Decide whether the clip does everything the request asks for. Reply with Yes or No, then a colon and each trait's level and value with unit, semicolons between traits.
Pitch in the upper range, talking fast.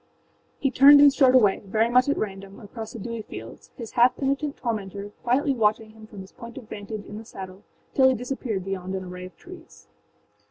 Yes: high, 225 Hz; fast, 210 wpm